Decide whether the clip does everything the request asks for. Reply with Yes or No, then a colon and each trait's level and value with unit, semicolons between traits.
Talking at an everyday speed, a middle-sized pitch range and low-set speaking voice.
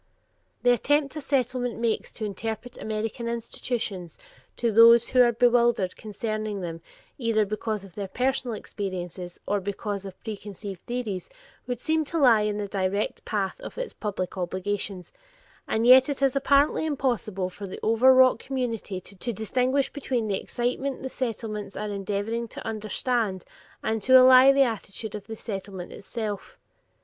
No: average, 155 wpm; average, 3.7 semitones; high, 220 Hz